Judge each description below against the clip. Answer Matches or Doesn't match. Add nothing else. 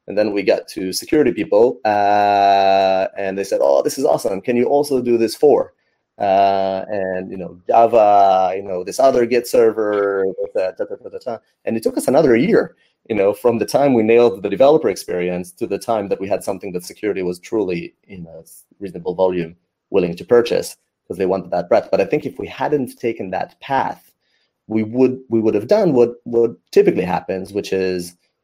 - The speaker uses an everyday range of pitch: Matches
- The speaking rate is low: Doesn't match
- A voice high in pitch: Doesn't match